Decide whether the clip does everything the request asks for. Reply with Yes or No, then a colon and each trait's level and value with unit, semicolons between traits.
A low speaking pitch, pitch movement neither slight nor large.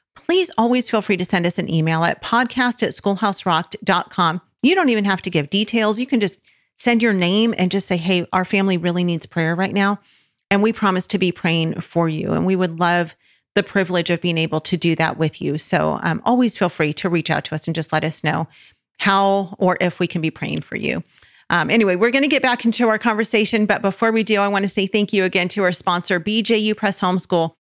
No: high, 190 Hz; average, 3.7 semitones